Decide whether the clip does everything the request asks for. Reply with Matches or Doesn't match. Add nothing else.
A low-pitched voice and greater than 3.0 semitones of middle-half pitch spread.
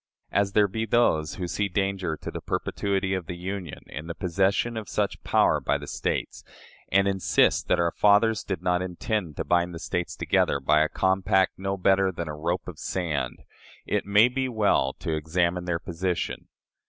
Doesn't match